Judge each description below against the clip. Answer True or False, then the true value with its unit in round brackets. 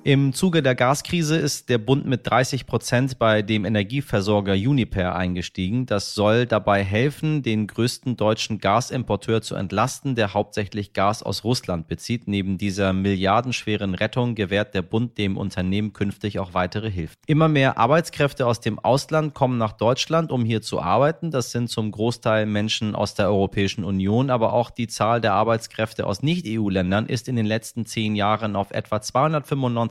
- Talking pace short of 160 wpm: False (165 wpm)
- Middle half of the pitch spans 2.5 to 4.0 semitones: True (3.7 semitones)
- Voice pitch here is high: False (110 Hz)